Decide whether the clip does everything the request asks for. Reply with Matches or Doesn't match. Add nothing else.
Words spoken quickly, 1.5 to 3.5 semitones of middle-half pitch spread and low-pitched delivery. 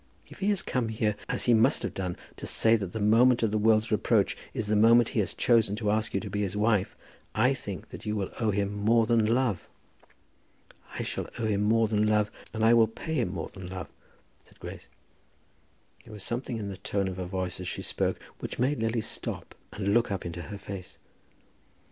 Matches